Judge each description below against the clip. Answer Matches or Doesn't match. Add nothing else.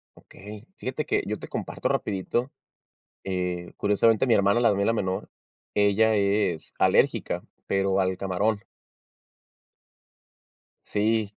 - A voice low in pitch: Matches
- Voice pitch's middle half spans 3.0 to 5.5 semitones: Doesn't match